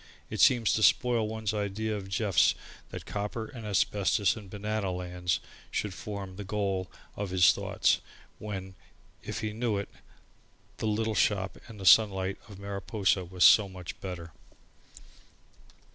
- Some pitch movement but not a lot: No, narrow, 2.2 semitones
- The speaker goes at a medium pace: Yes, average, 145 wpm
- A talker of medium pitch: No, low, 100 Hz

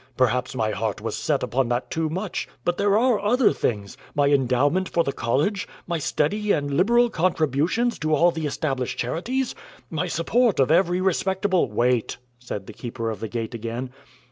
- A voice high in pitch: No, medium, 155 Hz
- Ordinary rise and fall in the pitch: No, wide, 7.2 semitones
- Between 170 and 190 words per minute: Yes, average, 180 wpm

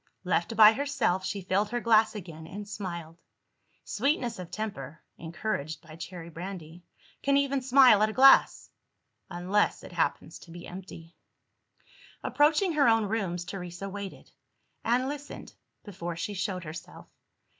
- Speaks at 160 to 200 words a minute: No, average, 140 wpm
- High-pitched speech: Yes, high, 200 Hz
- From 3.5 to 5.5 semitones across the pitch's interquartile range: Yes, average, 4.9 semitones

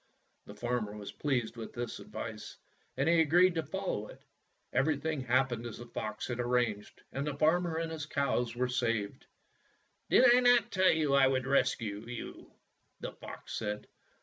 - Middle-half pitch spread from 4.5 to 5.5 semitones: Yes, average, 5.2 semitones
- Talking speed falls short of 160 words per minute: No, average, 175 wpm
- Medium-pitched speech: No, low, 130 Hz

